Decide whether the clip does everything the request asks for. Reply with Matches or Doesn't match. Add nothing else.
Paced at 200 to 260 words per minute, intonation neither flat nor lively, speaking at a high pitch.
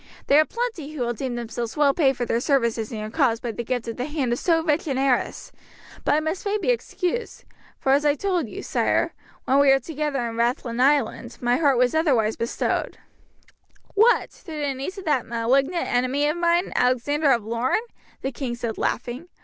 Matches